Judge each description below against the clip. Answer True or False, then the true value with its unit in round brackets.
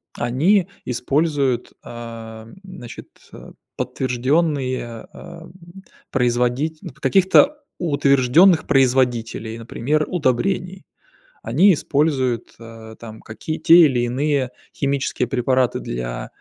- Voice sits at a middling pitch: False (130 Hz)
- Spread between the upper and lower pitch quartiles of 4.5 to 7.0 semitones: True (4.8 semitones)